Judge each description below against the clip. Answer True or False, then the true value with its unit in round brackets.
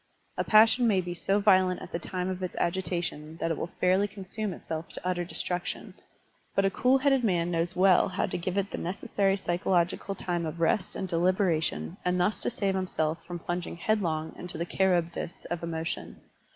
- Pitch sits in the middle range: True (180 Hz)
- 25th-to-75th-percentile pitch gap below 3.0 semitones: True (2.4 semitones)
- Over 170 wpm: True (195 wpm)